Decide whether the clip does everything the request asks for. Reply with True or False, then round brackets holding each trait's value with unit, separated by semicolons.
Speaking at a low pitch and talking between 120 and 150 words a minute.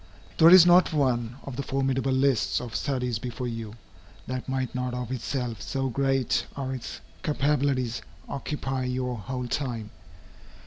True (130 Hz; 145 wpm)